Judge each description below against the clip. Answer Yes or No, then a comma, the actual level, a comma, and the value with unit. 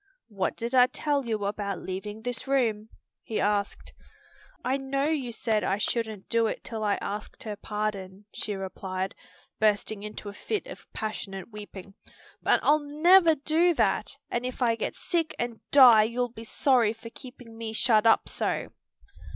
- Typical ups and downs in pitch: Yes, average, 3.7 semitones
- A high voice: Yes, high, 225 Hz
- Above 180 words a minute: No, average, 165 wpm